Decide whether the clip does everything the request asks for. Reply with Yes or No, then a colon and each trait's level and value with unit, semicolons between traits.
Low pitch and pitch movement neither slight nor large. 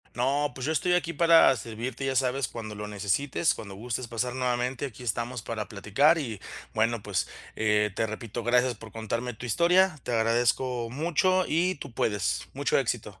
Yes: low, 120 Hz; average, 4.1 semitones